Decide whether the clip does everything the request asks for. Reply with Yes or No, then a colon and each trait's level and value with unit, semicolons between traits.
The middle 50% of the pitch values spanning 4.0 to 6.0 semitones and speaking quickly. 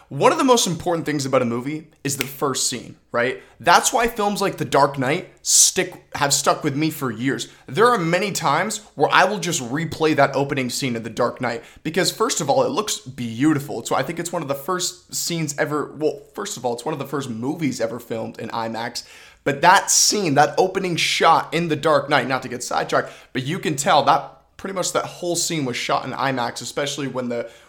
Yes: average, 4.6 semitones; fast, 225 wpm